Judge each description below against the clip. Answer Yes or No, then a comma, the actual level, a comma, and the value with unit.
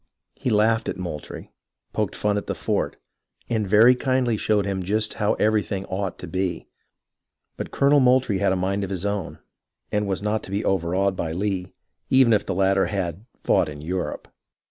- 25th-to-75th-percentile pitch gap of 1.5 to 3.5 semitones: Yes, narrow, 2.5 semitones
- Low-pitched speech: Yes, low, 100 Hz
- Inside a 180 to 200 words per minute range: Yes, average, 185 wpm